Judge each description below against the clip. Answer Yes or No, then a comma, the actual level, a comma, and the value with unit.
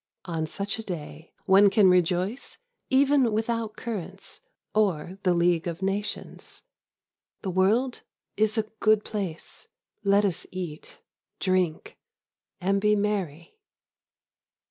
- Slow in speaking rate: Yes, slow, 115 wpm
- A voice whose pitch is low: No, high, 195 Hz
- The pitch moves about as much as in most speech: Yes, average, 3.3 semitones